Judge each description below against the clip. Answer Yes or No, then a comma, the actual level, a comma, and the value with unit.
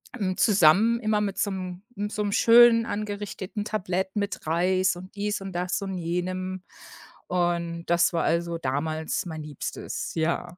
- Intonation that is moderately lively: Yes, average, 3.1 semitones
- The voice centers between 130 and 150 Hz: No, medium, 185 Hz